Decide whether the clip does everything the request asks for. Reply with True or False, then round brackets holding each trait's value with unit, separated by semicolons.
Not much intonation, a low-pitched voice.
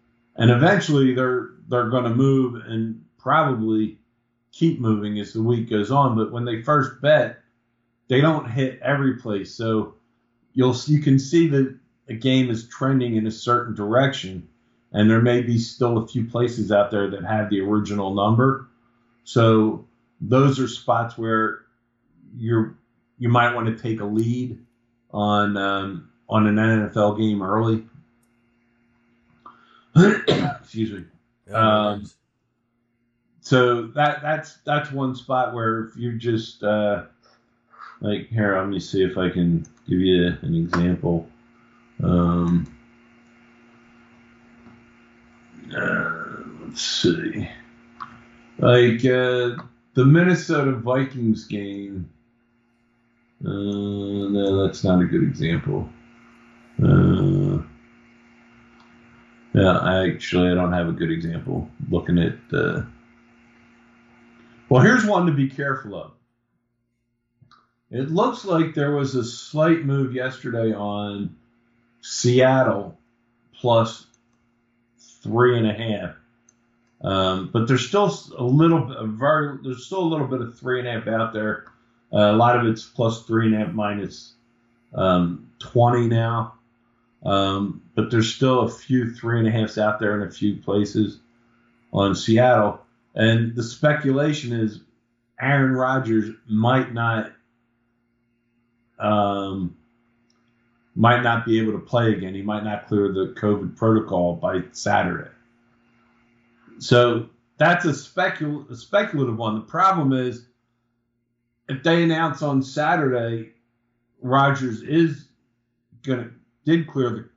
True (2.2 semitones; 120 Hz)